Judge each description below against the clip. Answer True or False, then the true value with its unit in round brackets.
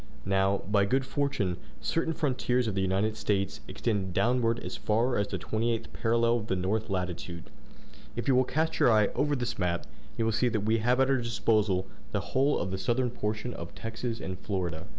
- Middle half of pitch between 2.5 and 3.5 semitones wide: False (4.0 semitones)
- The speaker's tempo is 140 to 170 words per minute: False (200 wpm)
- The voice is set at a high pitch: False (110 Hz)